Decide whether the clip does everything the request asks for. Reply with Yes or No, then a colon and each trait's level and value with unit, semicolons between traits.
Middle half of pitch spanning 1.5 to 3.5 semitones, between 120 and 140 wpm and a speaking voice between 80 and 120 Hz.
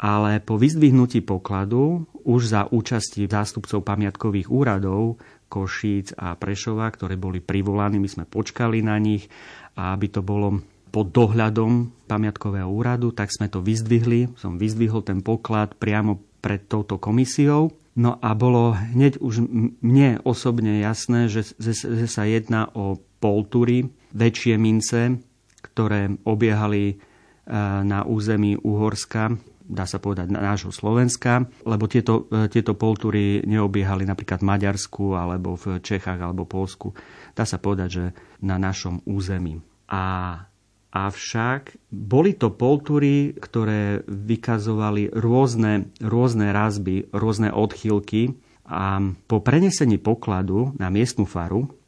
Yes: average, 2.7 semitones; average, 125 wpm; low, 105 Hz